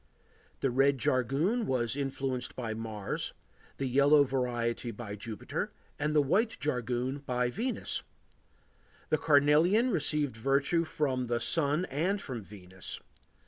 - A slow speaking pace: Yes, slow, 125 wpm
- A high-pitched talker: No, low, 135 Hz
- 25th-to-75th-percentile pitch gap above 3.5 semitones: Yes, average, 3.9 semitones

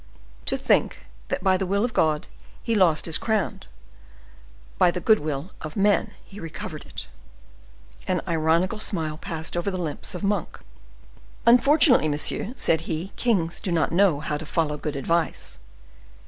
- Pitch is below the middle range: No, medium, 170 Hz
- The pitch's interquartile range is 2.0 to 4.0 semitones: No, average, 4.5 semitones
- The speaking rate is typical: Yes, average, 160 wpm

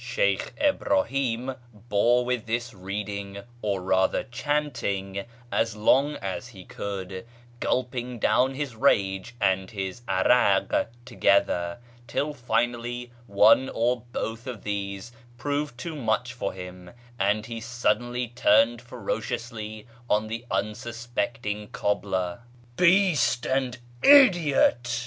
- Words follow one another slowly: Yes, slow, 115 wpm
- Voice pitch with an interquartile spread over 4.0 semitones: No, average, 3.7 semitones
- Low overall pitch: Yes, low, 115 Hz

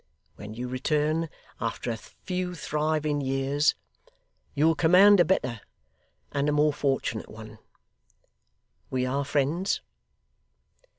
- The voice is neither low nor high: Yes, medium, 145 Hz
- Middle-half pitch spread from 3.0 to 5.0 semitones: Yes, average, 3.8 semitones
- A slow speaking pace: Yes, slow, 115 wpm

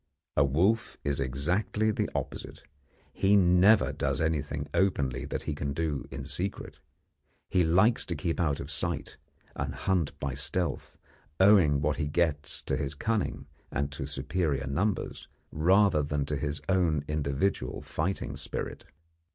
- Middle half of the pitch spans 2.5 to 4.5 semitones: No, average, 4.9 semitones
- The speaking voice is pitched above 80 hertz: No, very low, 75 Hz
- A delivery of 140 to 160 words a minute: Yes, average, 145 wpm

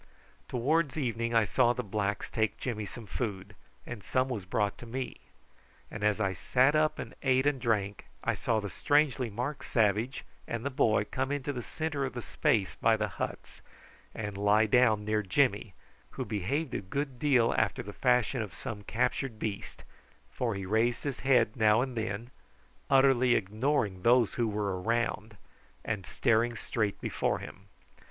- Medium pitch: No, low, 115 Hz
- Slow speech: No, average, 170 wpm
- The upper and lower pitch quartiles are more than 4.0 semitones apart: No, average, 3.7 semitones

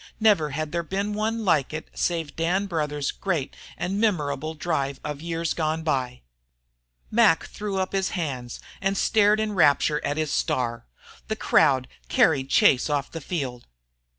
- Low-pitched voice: No, medium, 160 Hz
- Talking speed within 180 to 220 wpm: No, average, 155 wpm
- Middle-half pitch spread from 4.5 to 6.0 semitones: Yes, average, 5.2 semitones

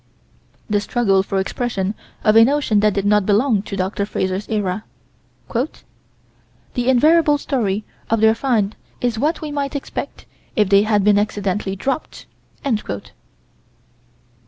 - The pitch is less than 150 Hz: No, high, 215 Hz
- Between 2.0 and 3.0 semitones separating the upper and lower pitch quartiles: No, average, 3.7 semitones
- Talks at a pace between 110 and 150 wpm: Yes, slow, 135 wpm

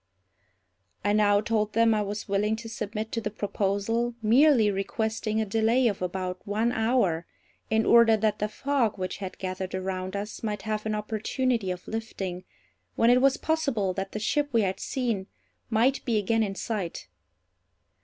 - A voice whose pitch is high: Yes, high, 215 Hz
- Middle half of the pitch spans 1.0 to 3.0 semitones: Yes, narrow, 2.6 semitones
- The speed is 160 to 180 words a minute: Yes, average, 170 wpm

